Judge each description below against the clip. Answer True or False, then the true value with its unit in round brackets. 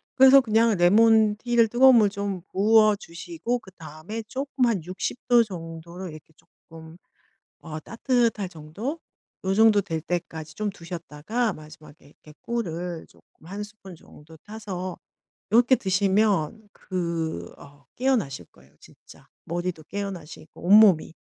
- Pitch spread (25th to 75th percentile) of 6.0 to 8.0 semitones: False (5.3 semitones)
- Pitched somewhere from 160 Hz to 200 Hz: True (190 Hz)